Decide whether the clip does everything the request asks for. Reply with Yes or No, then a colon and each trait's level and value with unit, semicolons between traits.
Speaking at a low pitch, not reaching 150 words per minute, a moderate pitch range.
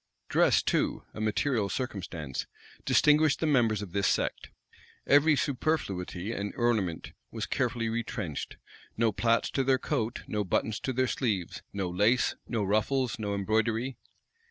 Yes: low, 110 Hz; average, 140 wpm; average, 4.2 semitones